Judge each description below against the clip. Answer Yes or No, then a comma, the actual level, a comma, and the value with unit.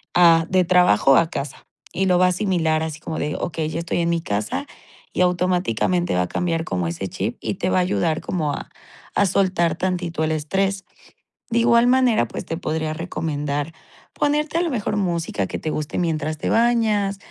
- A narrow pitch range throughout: No, average, 3.5 semitones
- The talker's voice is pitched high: No, medium, 170 Hz